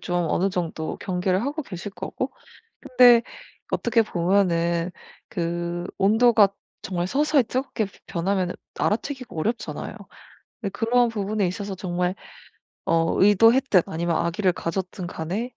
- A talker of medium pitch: No, high, 195 Hz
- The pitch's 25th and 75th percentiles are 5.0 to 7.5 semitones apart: No, average, 4.6 semitones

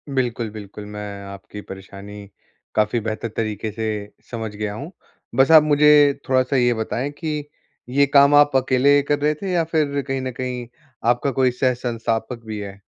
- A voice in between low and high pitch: No, low, 125 Hz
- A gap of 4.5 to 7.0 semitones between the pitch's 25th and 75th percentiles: Yes, average, 4.8 semitones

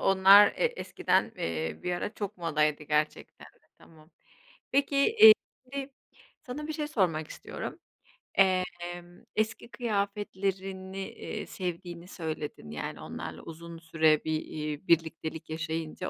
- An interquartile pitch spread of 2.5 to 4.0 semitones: No, average, 4.4 semitones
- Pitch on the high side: No, medium, 175 Hz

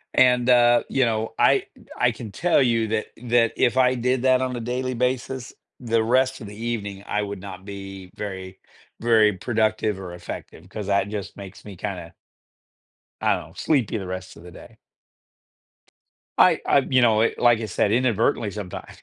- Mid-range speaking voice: No, low, 110 Hz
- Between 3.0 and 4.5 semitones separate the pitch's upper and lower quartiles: Yes, average, 3.6 semitones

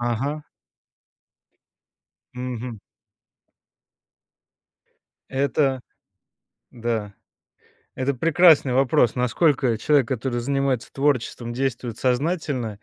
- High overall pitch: No, low, 130 Hz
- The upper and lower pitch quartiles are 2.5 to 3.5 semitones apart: Yes, average, 2.8 semitones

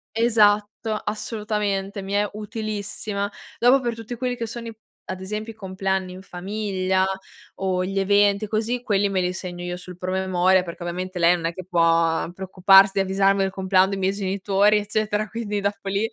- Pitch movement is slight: Yes, narrow, 2.2 semitones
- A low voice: No, high, 195 Hz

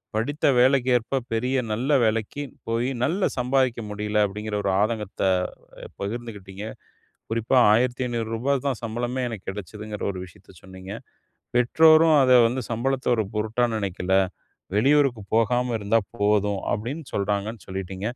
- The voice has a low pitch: Yes, low, 115 Hz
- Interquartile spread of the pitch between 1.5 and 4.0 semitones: Yes, average, 3.3 semitones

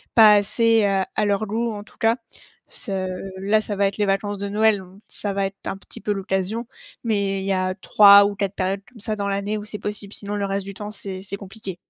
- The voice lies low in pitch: No, high, 200 Hz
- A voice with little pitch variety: Yes, narrow, 1.4 semitones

